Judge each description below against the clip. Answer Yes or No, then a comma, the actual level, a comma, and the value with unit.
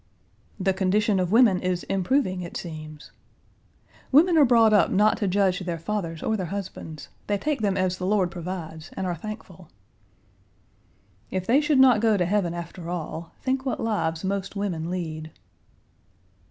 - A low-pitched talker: No, high, 190 Hz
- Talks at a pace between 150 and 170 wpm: Yes, average, 165 wpm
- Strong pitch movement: No, average, 3.6 semitones